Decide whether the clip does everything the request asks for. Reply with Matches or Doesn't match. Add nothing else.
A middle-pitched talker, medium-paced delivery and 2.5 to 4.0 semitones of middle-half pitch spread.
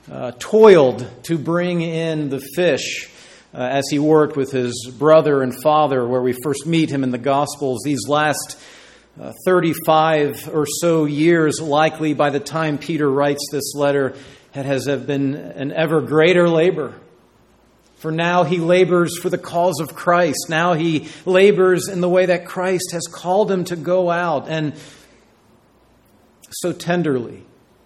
Matches